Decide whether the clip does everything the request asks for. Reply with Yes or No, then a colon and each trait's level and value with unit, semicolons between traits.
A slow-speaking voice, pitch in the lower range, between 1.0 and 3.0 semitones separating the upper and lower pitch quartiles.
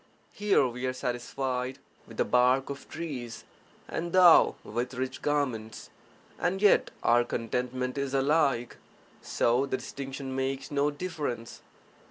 Yes: slow, 130 wpm; low, 130 Hz; narrow, 2.6 semitones